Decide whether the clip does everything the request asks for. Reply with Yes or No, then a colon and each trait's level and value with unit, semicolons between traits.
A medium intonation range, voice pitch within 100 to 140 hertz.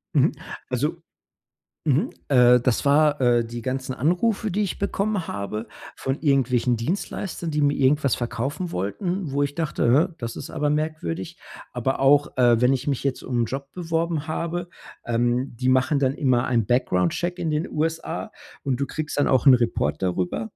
Yes: average, 4.4 semitones; low, 135 Hz